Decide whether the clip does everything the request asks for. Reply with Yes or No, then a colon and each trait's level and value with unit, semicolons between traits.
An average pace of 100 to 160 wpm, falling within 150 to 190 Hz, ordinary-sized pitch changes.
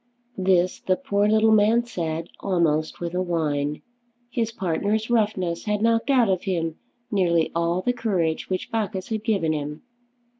Yes: average, 155 wpm; medium, 185 Hz; average, 4.5 semitones